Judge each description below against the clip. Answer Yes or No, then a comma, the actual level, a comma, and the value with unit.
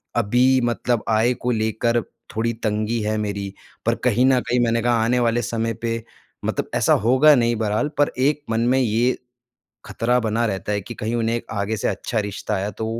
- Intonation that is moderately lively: No, narrow, 2.1 semitones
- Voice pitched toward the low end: Yes, low, 115 Hz